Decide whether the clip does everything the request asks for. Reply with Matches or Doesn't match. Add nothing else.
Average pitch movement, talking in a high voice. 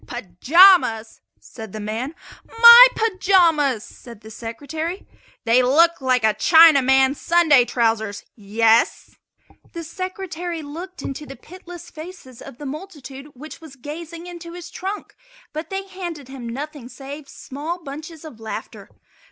Doesn't match